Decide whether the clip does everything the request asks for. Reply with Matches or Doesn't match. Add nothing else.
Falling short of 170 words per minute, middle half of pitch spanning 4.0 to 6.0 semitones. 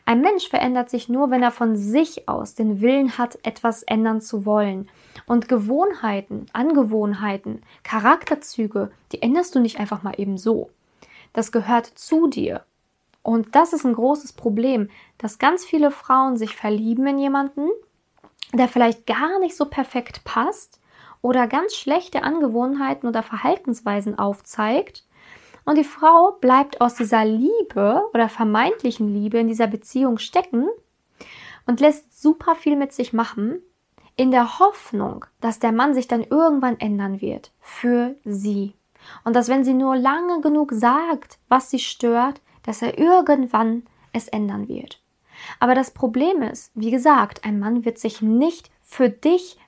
Matches